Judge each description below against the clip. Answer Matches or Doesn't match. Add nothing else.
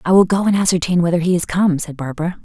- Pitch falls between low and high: Matches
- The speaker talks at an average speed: Doesn't match